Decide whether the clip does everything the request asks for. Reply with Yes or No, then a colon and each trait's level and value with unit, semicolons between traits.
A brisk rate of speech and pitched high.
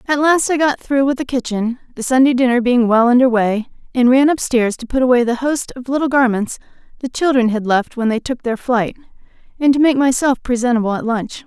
Yes: fast, 220 wpm; very high, 250 Hz